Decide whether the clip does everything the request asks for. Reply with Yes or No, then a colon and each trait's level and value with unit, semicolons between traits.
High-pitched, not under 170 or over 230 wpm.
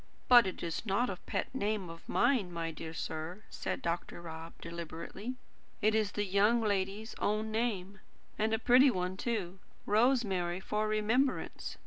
No: high, 205 Hz; average, 155 wpm